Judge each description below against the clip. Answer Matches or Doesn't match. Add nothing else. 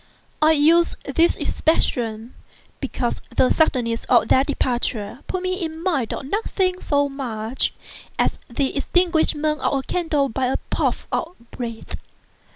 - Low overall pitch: Doesn't match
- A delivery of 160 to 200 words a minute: Doesn't match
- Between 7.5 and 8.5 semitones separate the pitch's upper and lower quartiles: Doesn't match